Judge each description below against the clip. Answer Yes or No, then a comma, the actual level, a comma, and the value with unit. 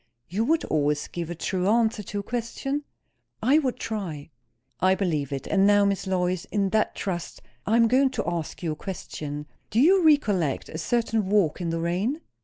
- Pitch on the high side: Yes, high, 195 Hz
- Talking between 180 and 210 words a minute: Yes, average, 195 wpm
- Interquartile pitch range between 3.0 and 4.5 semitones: No, average, 5.3 semitones